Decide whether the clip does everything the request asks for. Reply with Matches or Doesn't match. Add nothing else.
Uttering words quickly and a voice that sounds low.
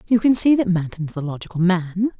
Doesn't match